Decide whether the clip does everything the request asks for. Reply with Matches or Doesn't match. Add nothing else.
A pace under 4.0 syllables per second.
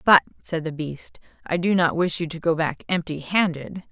Doesn't match